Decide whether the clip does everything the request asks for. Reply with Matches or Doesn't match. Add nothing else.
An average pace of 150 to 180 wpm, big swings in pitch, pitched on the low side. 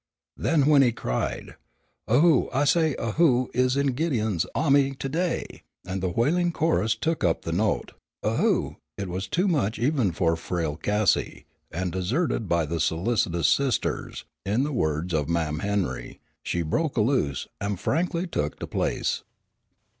Matches